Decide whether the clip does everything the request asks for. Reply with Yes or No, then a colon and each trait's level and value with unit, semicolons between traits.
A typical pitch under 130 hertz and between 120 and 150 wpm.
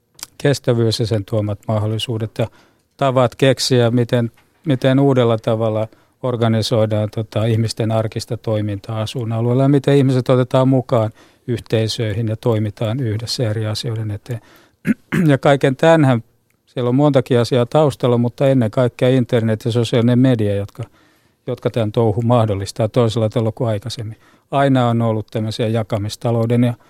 Yes: low, 120 Hz; average, 135 wpm